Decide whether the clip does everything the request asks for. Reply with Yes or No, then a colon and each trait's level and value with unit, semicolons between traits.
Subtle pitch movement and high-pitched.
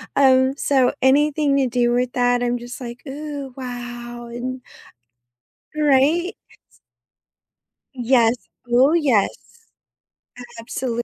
Yes: narrow, 2.3 semitones; very high, 255 Hz